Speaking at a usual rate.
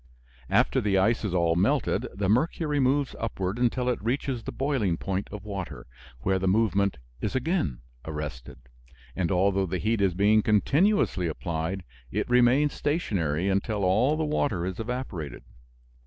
Yes: average, 155 wpm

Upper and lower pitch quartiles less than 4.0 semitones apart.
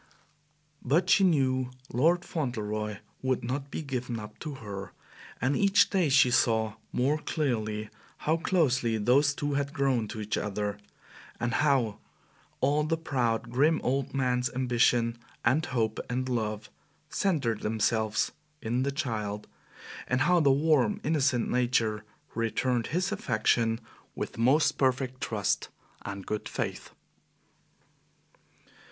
No: average, 4.3 semitones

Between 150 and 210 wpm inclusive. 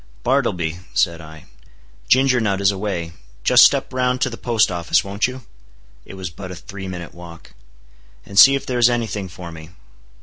Yes: average, 190 wpm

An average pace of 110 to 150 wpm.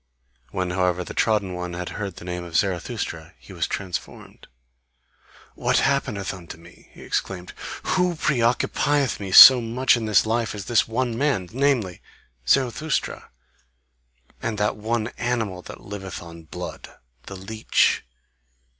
Yes: average, 140 wpm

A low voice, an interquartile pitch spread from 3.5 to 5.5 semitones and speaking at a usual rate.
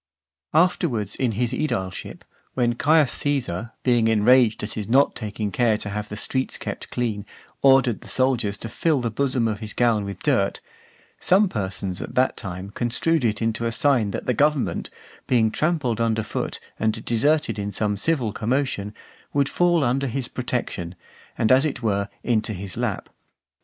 Yes: low, 115 Hz; average, 4.0 semitones; average, 170 wpm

